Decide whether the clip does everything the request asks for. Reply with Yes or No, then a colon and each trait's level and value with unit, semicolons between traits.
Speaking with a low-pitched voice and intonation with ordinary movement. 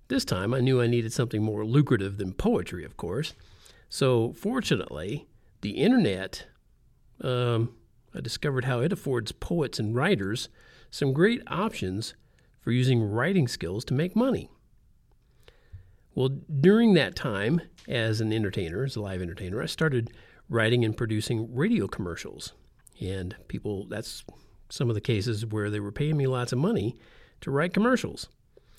Yes: low, 120 Hz; average, 4.4 semitones